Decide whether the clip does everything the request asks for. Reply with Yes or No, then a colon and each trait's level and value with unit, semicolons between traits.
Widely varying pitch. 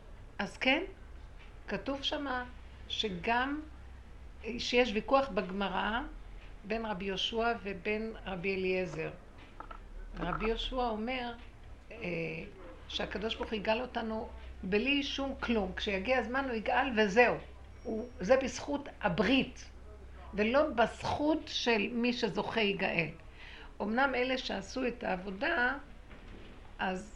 No: average, 3.9 semitones